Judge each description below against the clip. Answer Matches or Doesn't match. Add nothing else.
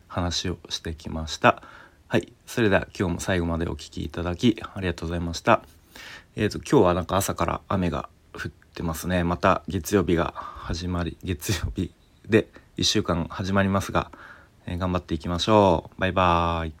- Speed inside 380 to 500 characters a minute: Doesn't match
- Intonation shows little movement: Matches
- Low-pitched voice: Matches